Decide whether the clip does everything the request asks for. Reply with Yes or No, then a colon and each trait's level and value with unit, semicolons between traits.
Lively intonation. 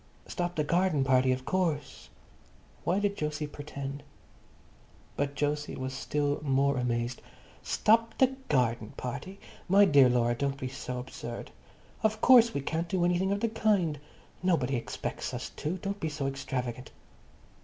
Yes: wide, 5.9 semitones